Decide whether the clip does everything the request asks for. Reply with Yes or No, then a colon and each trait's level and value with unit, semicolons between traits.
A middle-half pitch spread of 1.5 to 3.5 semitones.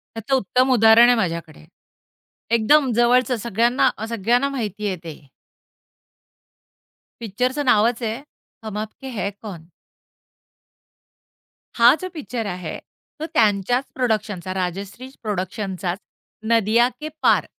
No: average, 4.0 semitones